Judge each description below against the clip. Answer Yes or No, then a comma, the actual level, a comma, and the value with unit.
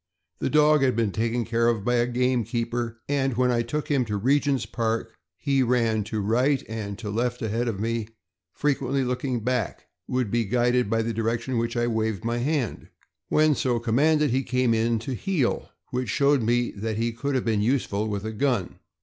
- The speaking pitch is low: Yes, low, 120 Hz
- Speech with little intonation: Yes, narrow, 2.3 semitones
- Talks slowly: No, average, 200 wpm